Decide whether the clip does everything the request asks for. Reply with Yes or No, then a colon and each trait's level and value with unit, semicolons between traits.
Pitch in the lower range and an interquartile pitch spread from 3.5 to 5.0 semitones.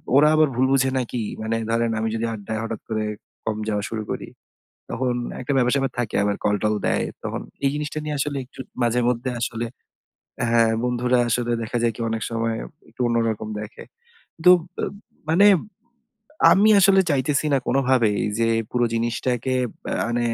No: low, 120 Hz; average, 2.7 semitones